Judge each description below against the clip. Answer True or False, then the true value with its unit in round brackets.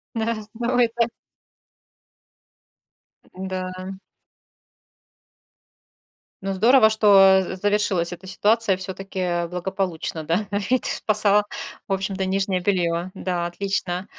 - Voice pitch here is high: True (195 Hz)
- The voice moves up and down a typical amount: False (2.2 semitones)